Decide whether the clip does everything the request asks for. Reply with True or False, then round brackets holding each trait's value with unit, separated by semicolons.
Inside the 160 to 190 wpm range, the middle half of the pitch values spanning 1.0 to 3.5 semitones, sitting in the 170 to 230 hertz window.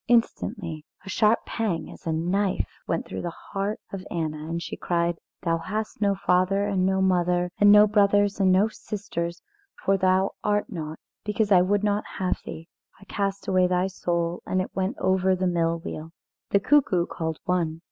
True (185 wpm; 2.9 semitones; 185 Hz)